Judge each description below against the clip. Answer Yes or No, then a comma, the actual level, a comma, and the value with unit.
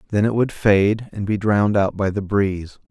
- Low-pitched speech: Yes, low, 100 Hz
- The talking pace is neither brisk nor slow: No, fast, 230 wpm